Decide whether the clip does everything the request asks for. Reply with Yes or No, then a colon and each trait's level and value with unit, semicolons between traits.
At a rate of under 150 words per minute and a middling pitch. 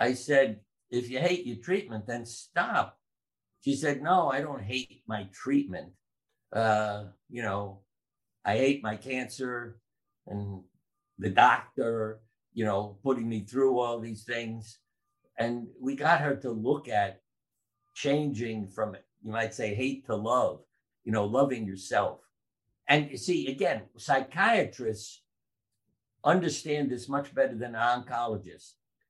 No: slow, 135 wpm; low, 120 Hz